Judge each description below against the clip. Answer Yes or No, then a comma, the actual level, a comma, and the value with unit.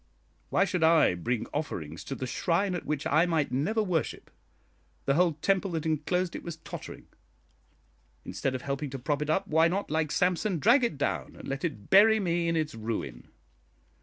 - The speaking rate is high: No, average, 190 wpm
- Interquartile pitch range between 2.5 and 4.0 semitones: No, average, 4.5 semitones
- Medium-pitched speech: Yes, medium, 160 Hz